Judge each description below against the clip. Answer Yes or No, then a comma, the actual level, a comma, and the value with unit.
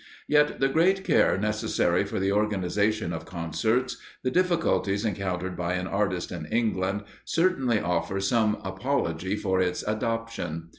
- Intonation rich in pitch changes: No, average, 4.0 semitones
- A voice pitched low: Yes, low, 100 Hz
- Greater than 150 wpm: No, average, 140 wpm